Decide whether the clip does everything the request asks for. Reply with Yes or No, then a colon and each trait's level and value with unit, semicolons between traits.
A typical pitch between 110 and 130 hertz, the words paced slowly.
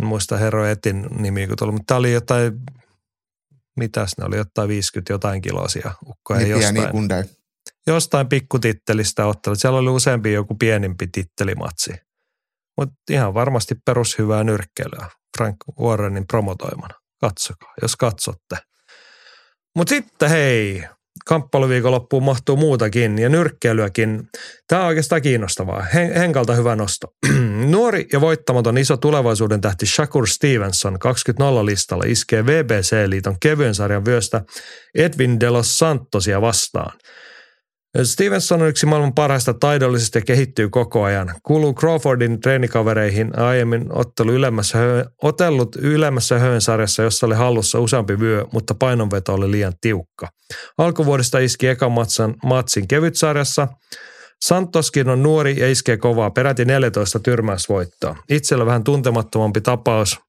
No: low, 120 Hz; average, 120 wpm